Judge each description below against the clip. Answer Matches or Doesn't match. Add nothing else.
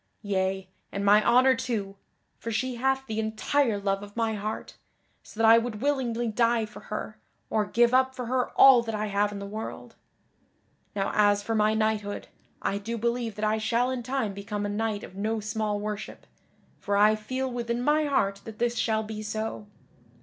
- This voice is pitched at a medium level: Doesn't match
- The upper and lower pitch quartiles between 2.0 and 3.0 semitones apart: Matches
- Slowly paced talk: Doesn't match